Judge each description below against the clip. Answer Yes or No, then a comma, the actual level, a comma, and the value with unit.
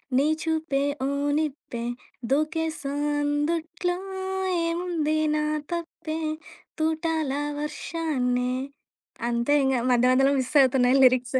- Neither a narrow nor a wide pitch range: Yes, average, 3.6 semitones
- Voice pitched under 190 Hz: No, very high, 295 Hz